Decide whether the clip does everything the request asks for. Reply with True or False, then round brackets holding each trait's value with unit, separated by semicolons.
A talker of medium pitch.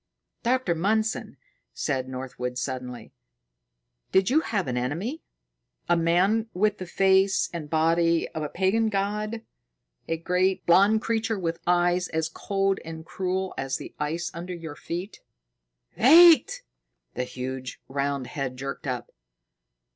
True (175 Hz)